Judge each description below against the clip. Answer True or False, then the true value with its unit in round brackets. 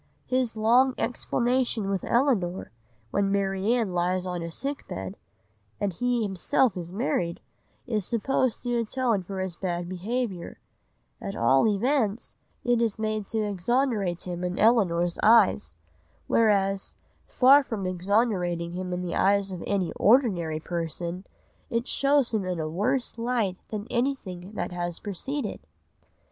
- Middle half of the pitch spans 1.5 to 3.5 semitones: False (5.0 semitones)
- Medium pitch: False (200 Hz)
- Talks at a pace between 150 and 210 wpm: False (140 wpm)